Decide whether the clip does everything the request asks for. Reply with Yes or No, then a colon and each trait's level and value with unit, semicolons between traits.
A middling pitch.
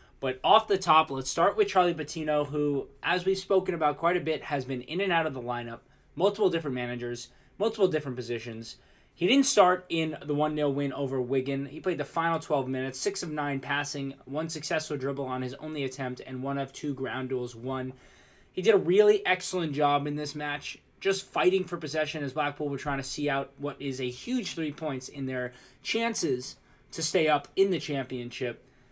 Yes: medium, 145 Hz